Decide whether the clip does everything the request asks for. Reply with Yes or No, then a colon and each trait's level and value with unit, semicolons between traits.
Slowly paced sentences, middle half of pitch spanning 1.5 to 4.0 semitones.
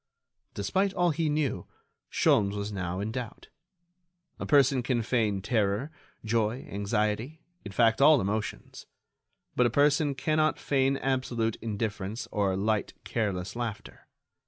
No: slow, 130 wpm; average, 4.8 semitones